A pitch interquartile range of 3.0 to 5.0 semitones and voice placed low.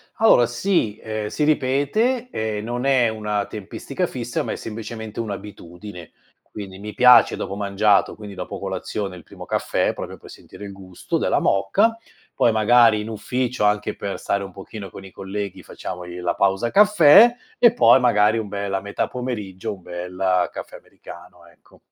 Yes: average, 3.9 semitones; low, 105 Hz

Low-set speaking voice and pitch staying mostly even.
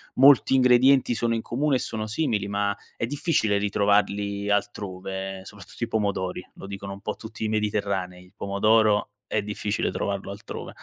Yes: low, 105 Hz; narrow, 2.2 semitones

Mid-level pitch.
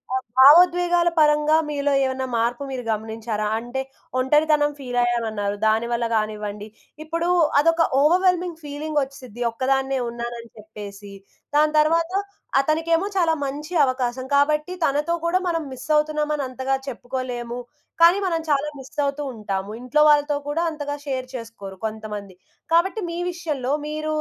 No: very high, 275 Hz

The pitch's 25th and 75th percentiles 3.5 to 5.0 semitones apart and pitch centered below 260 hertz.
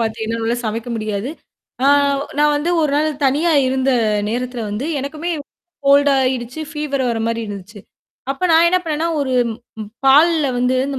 No: average, 4.5 semitones; very high, 265 Hz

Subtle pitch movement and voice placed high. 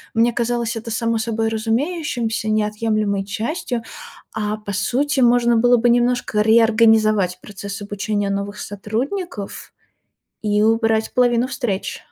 Yes: narrow, 2.3 semitones; high, 225 Hz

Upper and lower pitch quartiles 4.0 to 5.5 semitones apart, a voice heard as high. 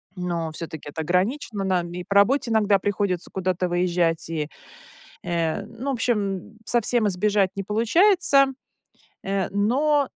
Yes: average, 4.4 semitones; high, 195 Hz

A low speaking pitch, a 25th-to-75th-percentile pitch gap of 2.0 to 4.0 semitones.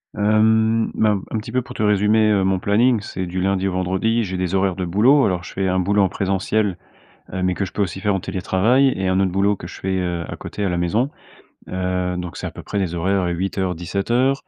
Yes: very low, 95 Hz; narrow, 2.6 semitones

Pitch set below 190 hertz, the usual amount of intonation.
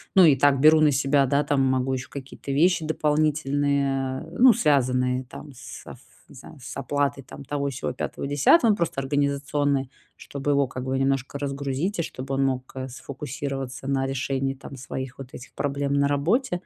No: medium, 140 Hz; narrow, 1.5 semitones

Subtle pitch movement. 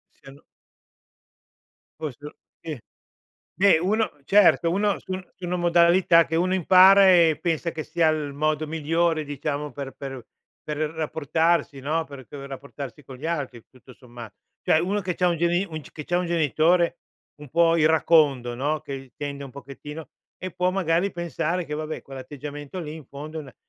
No: average, 3.4 semitones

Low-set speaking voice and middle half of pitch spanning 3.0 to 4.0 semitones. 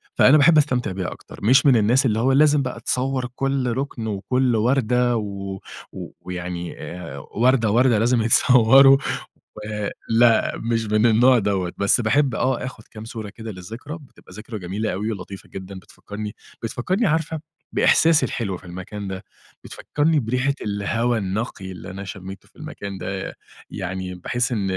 No: low, 115 Hz; average, 4.7 semitones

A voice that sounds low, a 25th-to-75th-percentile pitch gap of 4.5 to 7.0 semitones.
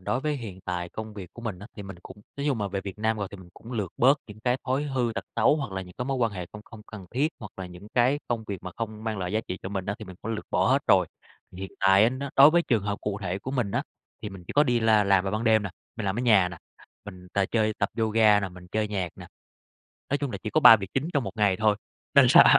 No: low, 105 Hz; average, 3.7 semitones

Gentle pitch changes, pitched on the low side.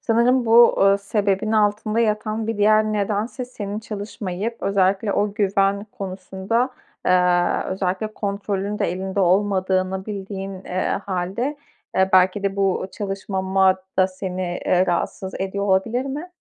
No: narrow, 2.1 semitones; high, 200 Hz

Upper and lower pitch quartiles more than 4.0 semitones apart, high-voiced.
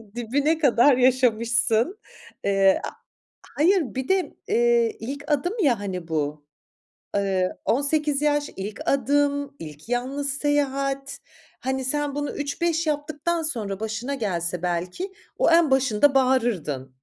Yes: average, 5.3 semitones; very high, 270 Hz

